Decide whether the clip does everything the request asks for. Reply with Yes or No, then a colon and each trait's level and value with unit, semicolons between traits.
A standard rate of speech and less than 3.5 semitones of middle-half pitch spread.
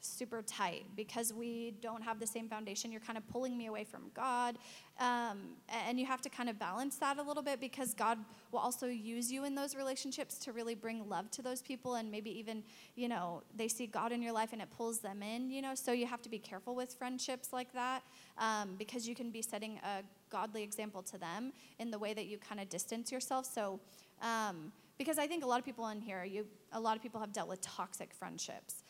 No: fast, 235 wpm; average, 2.8 semitones